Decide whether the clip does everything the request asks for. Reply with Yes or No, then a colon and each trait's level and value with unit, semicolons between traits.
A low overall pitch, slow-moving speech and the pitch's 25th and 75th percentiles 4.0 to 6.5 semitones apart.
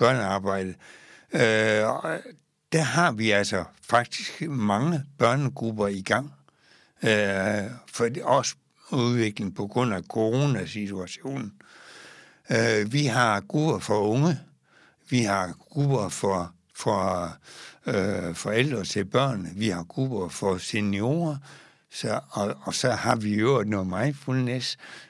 Yes: low, 115 Hz; slow, 120 wpm; average, 5.1 semitones